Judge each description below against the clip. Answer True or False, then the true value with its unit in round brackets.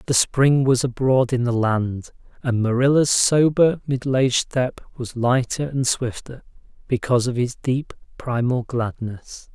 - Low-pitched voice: True (125 Hz)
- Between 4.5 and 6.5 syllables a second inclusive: False (4.3 syllables/s)